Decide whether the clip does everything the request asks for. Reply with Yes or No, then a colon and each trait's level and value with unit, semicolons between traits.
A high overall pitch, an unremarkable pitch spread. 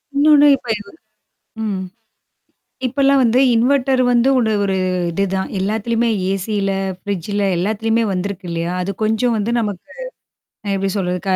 Yes: high, 210 Hz; average, 3.5 semitones